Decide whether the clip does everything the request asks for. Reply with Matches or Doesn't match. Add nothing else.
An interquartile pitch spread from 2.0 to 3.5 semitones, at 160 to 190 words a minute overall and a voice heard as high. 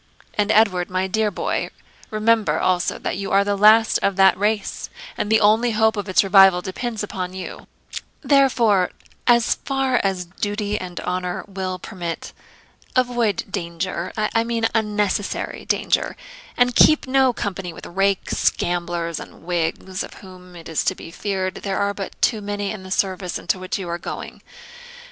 Matches